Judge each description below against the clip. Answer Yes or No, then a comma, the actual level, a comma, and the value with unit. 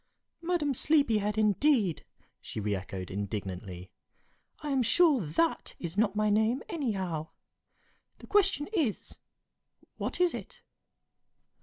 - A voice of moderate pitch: No, high, 215 Hz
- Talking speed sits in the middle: No, slow, 115 wpm